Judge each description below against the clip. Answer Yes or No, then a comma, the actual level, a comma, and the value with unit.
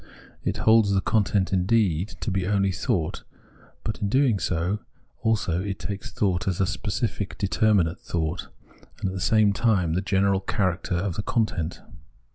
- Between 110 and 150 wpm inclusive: No, average, 165 wpm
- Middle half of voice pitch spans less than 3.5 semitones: Yes, average, 2.7 semitones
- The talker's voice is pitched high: No, very low, 95 Hz